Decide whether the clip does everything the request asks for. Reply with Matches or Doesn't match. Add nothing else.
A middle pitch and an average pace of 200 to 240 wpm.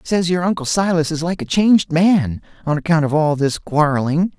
Matches